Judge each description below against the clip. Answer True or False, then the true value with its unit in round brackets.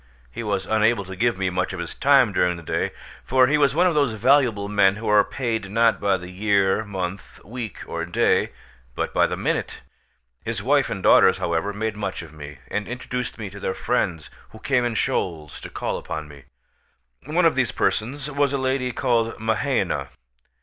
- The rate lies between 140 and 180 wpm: False (200 wpm)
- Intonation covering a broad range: False (4.8 semitones)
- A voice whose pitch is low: True (110 Hz)